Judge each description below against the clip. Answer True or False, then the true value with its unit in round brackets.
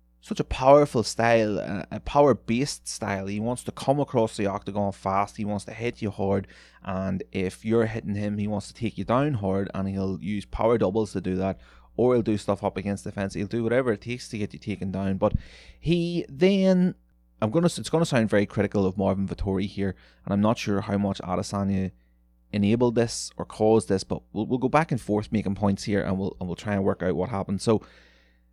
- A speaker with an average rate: False (225 wpm)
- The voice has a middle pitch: False (100 Hz)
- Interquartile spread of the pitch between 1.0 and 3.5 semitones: True (2.8 semitones)